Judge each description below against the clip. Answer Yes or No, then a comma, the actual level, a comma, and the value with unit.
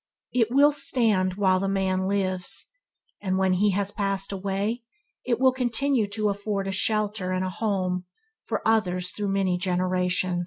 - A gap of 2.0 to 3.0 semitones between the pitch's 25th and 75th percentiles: Yes, narrow, 2.5 semitones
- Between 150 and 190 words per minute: Yes, average, 155 wpm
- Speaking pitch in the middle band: No, high, 195 Hz